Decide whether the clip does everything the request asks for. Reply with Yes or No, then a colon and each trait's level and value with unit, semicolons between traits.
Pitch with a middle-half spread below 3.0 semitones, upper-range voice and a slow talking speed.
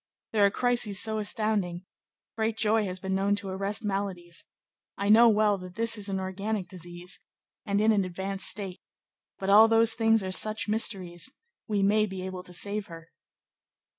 No: narrow, 2.5 semitones; high, 200 Hz; average, 175 wpm